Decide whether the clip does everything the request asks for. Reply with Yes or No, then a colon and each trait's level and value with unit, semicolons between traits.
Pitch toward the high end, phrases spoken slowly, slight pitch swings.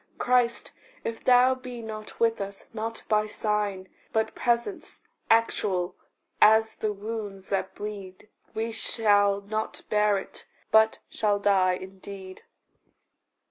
Yes: high, 215 Hz; slow, 120 wpm; narrow, 2.2 semitones